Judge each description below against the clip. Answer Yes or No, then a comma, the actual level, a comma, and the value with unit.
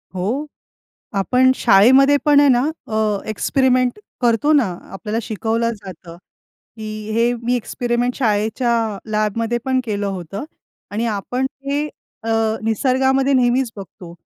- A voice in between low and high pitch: No, high, 235 Hz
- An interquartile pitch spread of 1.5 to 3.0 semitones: No, average, 3.5 semitones